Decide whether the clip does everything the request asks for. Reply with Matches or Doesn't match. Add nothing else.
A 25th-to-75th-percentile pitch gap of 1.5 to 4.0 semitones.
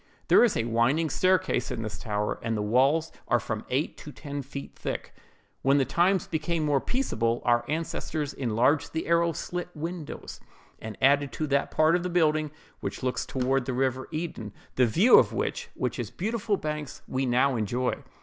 Doesn't match